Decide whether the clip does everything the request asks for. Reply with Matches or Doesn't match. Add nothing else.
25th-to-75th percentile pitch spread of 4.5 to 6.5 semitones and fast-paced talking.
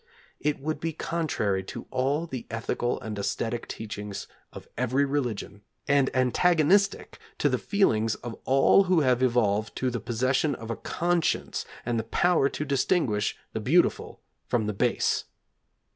Doesn't match